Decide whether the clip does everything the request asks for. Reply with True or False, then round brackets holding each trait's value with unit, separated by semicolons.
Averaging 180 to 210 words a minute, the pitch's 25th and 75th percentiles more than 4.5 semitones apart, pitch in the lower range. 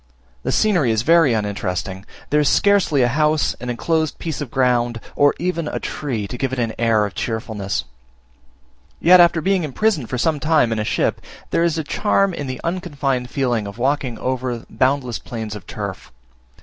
True (185 wpm; 5.5 semitones; 130 Hz)